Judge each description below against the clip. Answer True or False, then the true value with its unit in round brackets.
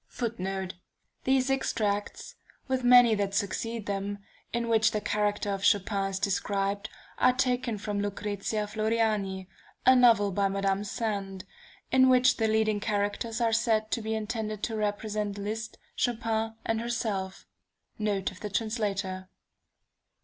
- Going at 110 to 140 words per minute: True (135 wpm)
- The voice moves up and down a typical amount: False (2.2 semitones)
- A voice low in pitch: False (215 Hz)